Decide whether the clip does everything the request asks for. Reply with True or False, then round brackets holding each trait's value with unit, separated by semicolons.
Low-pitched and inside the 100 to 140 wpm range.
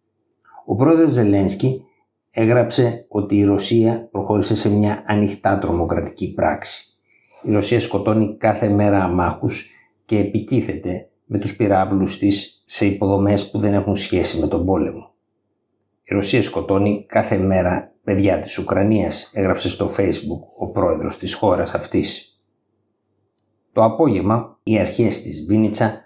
True (105 Hz; 130 wpm)